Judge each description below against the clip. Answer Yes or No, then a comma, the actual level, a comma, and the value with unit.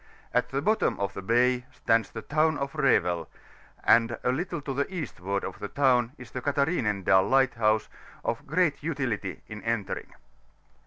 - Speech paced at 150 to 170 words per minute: Yes, average, 160 wpm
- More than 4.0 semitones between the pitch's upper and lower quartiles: Yes, average, 4.8 semitones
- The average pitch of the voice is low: Yes, low, 125 Hz